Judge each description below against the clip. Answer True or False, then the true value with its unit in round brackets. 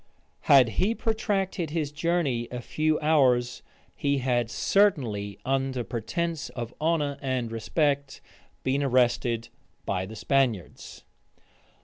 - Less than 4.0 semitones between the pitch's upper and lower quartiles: False (4.5 semitones)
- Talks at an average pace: False (110 wpm)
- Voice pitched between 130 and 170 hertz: True (135 Hz)